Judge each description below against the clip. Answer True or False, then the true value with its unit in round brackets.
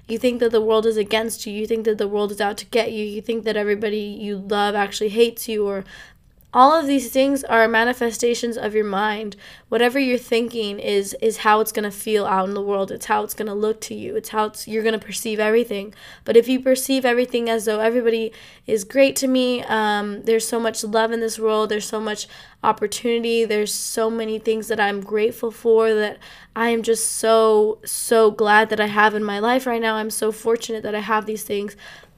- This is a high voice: True (220 Hz)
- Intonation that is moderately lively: False (1.5 semitones)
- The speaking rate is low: False (225 wpm)